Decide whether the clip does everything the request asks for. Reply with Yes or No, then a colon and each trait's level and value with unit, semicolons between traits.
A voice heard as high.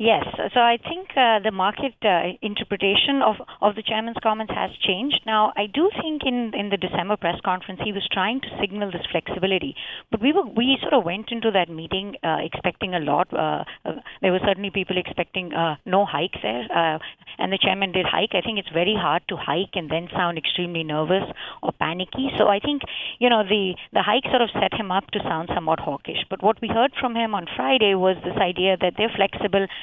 Yes: high, 200 Hz